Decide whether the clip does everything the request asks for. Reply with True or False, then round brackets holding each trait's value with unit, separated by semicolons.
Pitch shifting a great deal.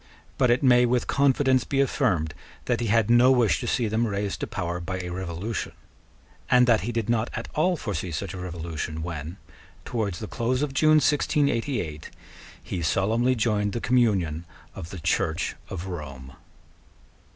True (6.0 semitones)